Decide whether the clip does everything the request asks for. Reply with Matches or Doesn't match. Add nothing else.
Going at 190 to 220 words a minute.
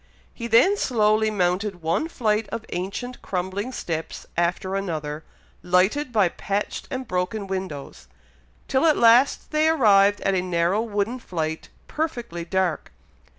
Doesn't match